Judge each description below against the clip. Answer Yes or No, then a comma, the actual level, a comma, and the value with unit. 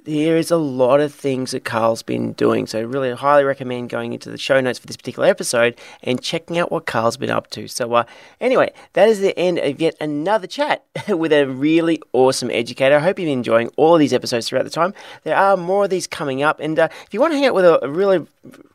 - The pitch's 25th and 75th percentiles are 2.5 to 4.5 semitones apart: No, wide, 5.5 semitones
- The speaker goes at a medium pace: No, fast, 250 wpm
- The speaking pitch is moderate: Yes, medium, 150 Hz